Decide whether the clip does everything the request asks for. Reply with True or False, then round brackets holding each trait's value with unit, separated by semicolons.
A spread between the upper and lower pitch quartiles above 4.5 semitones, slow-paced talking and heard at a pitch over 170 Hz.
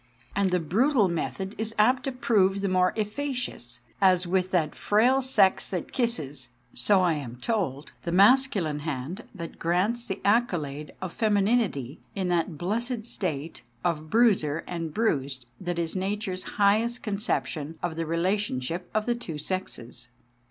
False (5.1 semitones; 150 wpm; 185 Hz)